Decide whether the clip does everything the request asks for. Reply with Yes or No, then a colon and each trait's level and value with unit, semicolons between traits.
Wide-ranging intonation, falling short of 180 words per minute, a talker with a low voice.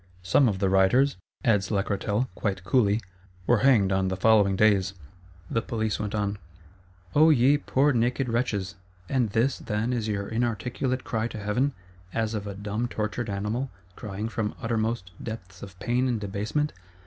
No: average, 3.3 semitones; average, 160 wpm; low, 110 Hz